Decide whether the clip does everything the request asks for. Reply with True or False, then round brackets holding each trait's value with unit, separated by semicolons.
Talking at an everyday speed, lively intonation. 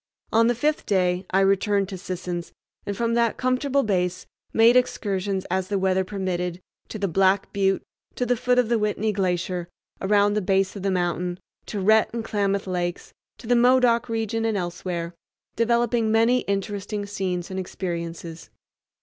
False (165 wpm; 3.5 semitones)